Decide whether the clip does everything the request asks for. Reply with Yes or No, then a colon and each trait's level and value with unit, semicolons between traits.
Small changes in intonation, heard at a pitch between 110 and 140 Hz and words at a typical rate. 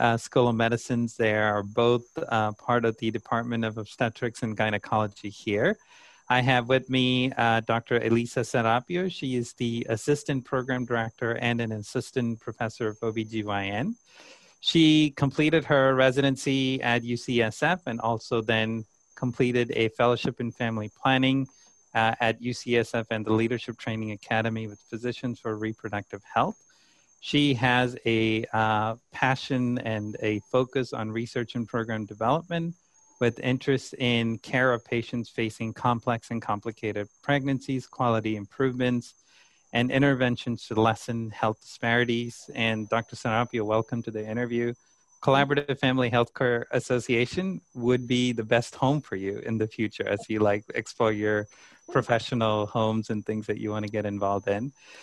Yes: narrow, 2.3 semitones; low, 120 Hz; average, 145 wpm